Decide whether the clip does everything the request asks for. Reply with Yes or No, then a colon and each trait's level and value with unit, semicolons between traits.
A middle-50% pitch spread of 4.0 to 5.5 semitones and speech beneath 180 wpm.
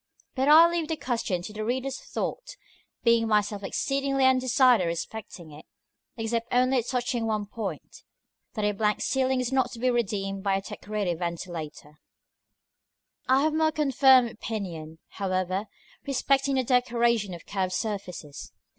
Yes: average, 5.0 semitones; average, 155 wpm